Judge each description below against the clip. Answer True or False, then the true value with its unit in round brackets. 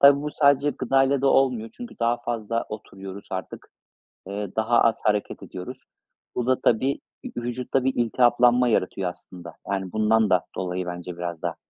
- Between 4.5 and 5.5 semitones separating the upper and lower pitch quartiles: True (4.9 semitones)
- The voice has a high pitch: False (115 Hz)